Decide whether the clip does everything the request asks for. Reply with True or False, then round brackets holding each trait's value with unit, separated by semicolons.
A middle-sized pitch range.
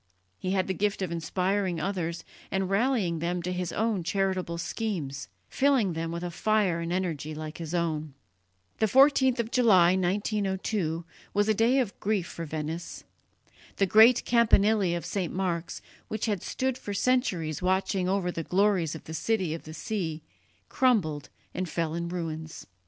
True (3.9 semitones)